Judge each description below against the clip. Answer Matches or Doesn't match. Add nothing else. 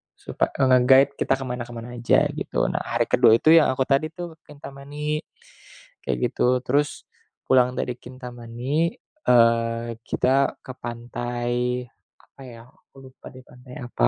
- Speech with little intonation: Matches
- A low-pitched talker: Matches